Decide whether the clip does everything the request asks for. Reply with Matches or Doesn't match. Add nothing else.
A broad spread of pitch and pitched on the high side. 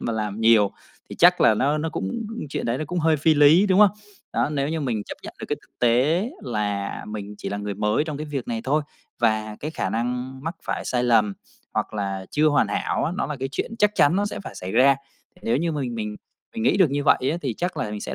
Doesn't match